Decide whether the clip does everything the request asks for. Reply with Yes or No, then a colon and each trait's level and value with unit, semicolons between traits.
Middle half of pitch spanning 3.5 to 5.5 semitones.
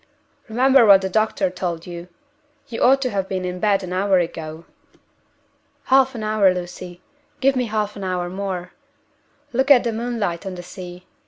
Yes: average, 4.0 semitones